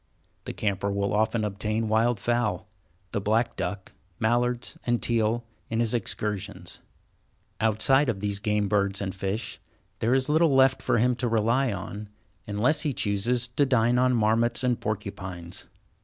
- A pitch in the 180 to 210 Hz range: No, low, 110 Hz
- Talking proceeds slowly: No, average, 155 wpm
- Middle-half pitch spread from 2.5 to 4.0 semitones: Yes, average, 3.0 semitones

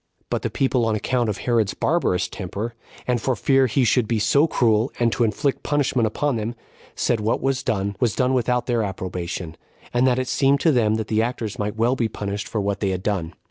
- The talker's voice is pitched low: Yes, low, 115 Hz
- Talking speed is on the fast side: Yes, fast, 225 wpm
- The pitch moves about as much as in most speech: Yes, average, 3.4 semitones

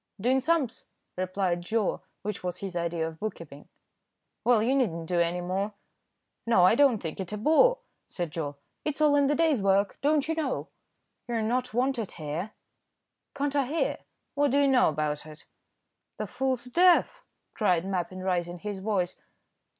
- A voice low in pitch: No, high, 210 Hz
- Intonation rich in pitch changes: Yes, wide, 7.2 semitones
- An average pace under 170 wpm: No, average, 175 wpm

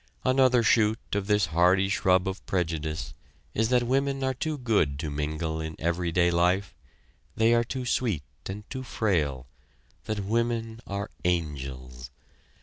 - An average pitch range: No, wide, 6.5 semitones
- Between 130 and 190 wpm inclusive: Yes, average, 145 wpm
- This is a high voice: No, very low, 95 Hz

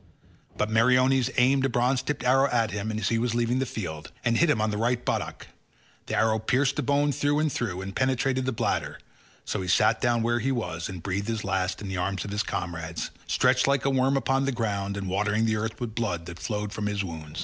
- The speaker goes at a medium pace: No, fast, 240 wpm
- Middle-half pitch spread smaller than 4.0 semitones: No, average, 4.5 semitones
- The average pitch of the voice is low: Yes, low, 115 Hz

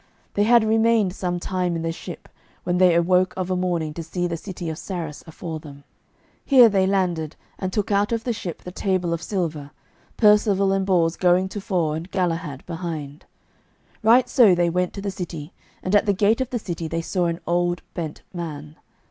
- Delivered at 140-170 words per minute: No, average, 200 wpm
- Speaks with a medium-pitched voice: Yes, medium, 180 Hz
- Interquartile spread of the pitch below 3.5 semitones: Yes, average, 3.1 semitones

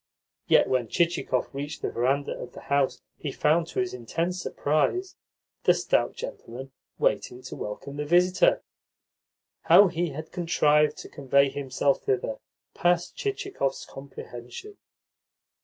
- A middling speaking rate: No, slow, 130 wpm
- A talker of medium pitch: Yes, medium, 145 Hz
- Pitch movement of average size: Yes, average, 4.7 semitones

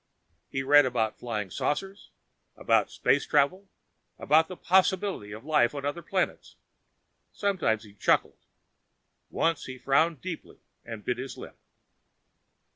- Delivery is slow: Yes, slow, 125 wpm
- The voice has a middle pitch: Yes, medium, 145 Hz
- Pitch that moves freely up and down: Yes, wide, 6.3 semitones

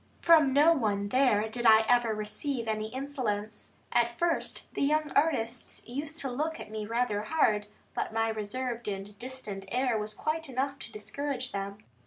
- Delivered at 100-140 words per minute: No, average, 170 wpm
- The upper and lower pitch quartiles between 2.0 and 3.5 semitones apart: No, average, 4.5 semitones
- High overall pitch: Yes, high, 240 Hz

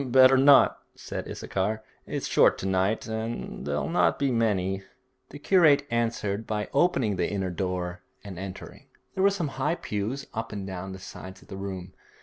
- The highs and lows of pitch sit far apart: Yes, wide, 5.7 semitones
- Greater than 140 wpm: Yes, average, 175 wpm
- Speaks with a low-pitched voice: Yes, low, 105 Hz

